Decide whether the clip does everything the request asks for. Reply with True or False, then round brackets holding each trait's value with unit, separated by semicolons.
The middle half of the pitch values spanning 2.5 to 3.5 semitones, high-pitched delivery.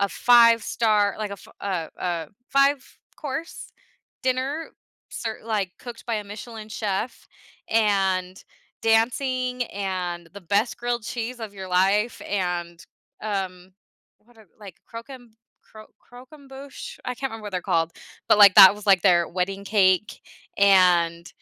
False (4.2 semitones; 210 Hz)